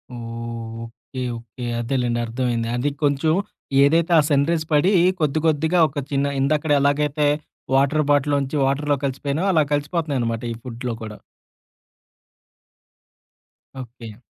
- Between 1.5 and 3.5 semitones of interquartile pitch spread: No, average, 3.9 semitones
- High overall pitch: No, medium, 140 Hz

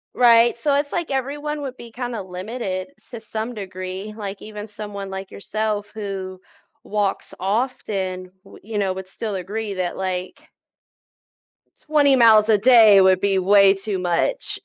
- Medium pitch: No, high, 210 Hz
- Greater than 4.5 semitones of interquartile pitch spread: No, average, 3.5 semitones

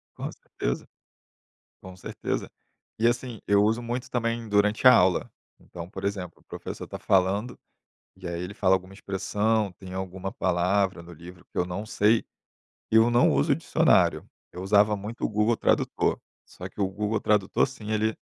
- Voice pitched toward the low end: Yes, low, 100 Hz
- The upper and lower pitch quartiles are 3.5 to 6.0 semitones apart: No, average, 3.0 semitones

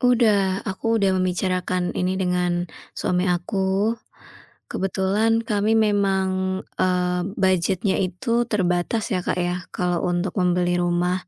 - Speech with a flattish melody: Yes, narrow, 2.1 semitones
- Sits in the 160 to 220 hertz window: Yes, medium, 185 Hz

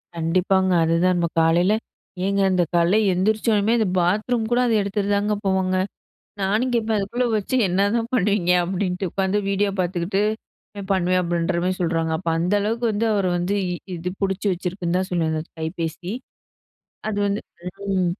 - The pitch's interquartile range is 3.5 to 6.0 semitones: No, average, 2.8 semitones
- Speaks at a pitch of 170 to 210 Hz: Yes, high, 190 Hz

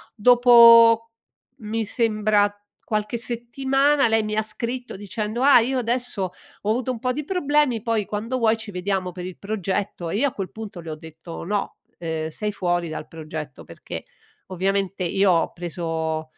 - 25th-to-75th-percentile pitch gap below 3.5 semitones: No, average, 4.6 semitones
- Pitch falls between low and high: No, high, 210 Hz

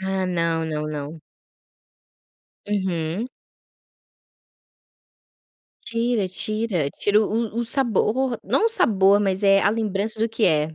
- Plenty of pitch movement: No, average, 5.0 semitones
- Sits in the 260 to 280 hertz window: No, high, 195 Hz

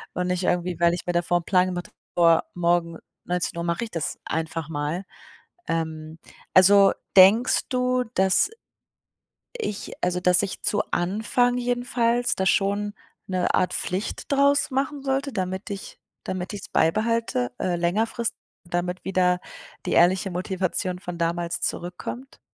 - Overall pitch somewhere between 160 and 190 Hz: Yes, medium, 185 Hz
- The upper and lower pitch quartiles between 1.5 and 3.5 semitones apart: No, average, 3.9 semitones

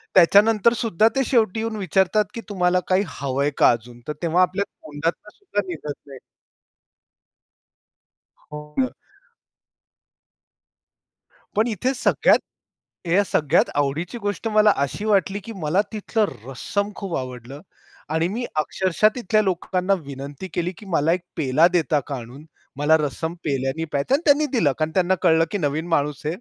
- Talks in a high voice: No, medium, 175 Hz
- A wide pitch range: Yes, wide, 5.8 semitones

